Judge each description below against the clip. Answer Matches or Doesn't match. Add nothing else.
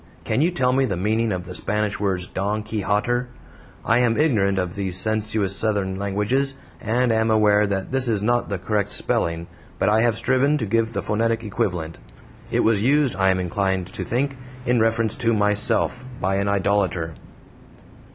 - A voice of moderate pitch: Doesn't match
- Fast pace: Doesn't match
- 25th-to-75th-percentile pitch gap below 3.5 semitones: Matches